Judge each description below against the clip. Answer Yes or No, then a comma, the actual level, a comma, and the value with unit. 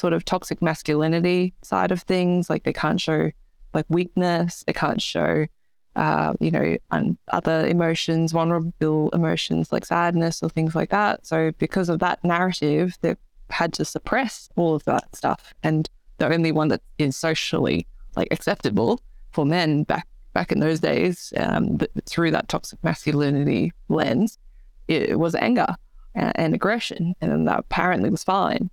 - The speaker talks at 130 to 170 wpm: Yes, average, 165 wpm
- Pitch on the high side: No, medium, 165 Hz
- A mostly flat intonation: Yes, narrow, 2.2 semitones